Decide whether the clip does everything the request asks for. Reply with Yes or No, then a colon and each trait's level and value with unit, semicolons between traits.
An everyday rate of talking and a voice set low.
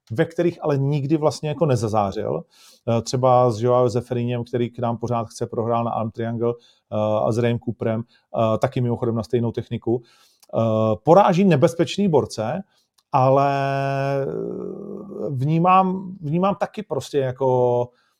Yes: average, 125 wpm; low, 125 Hz